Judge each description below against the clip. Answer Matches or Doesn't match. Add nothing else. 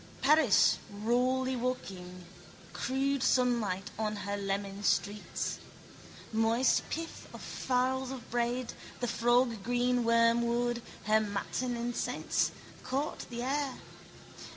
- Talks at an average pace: Doesn't match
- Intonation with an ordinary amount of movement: Matches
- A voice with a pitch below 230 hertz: Doesn't match